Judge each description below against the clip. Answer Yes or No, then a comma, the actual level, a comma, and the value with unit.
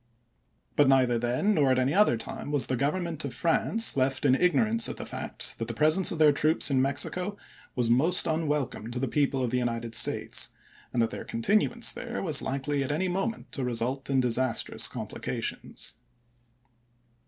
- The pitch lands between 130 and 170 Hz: Yes, medium, 140 Hz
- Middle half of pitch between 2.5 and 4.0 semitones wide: No, average, 4.8 semitones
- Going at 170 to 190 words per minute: Yes, average, 185 wpm